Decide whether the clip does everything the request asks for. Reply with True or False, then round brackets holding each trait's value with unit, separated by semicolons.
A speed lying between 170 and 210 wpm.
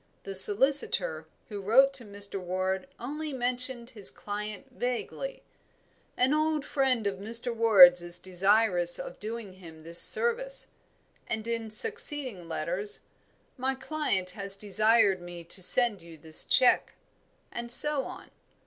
False (135 wpm)